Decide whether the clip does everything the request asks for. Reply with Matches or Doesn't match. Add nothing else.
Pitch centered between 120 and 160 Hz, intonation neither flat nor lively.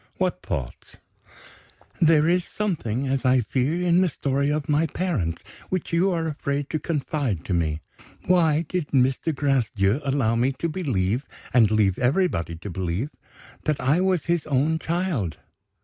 Doesn't match